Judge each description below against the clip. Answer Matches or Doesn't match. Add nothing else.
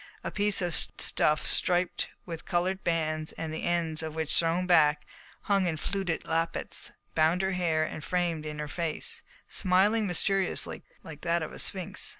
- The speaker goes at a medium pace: Matches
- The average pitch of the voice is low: Doesn't match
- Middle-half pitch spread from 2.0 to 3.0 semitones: Matches